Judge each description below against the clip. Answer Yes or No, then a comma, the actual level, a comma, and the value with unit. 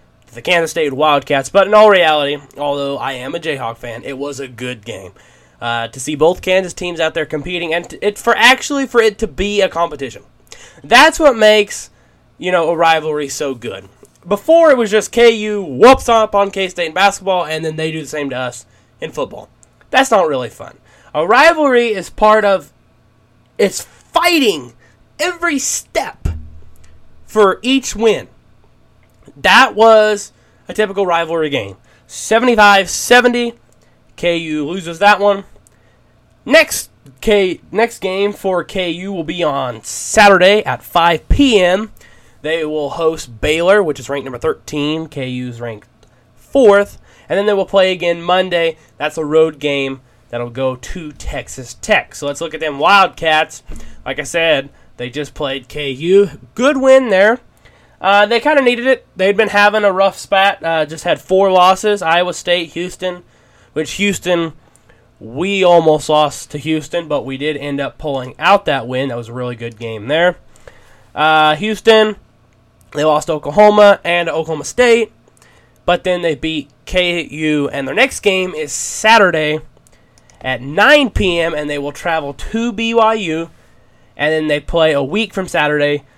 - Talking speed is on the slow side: No, average, 160 wpm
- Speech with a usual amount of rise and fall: No, wide, 6.0 semitones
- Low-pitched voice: No, medium, 165 Hz